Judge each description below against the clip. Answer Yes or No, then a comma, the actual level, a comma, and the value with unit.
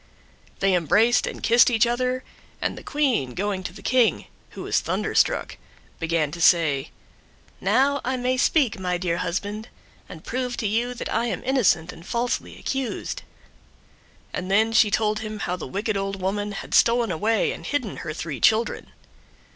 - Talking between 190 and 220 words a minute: No, average, 170 wpm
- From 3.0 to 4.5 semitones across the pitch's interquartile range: No, average, 5.0 semitones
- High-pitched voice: Yes, high, 215 Hz